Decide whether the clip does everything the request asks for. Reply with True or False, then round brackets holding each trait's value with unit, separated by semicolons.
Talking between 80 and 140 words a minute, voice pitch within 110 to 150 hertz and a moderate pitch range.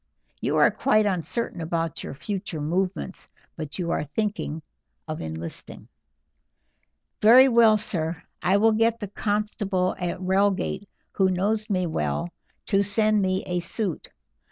False (135 wpm; 190 Hz; 3.9 semitones)